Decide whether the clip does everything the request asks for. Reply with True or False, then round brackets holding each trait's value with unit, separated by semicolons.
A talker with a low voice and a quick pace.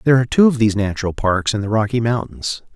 True (110 Hz; 240 wpm)